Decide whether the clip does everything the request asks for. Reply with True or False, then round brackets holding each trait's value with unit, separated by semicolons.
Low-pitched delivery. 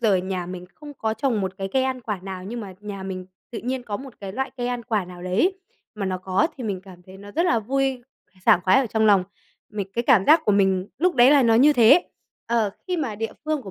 False (220 Hz)